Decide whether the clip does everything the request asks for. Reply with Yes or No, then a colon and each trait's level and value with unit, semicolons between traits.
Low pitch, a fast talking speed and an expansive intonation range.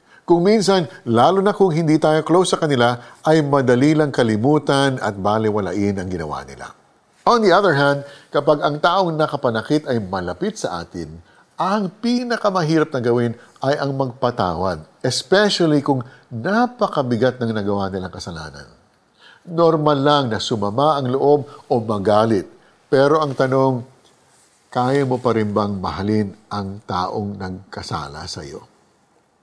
No: low, 130 Hz; average, 135 wpm; wide, 6.5 semitones